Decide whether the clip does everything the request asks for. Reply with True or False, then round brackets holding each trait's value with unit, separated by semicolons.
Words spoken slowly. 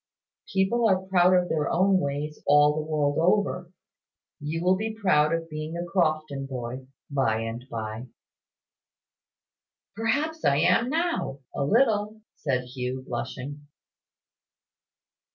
True (125 wpm)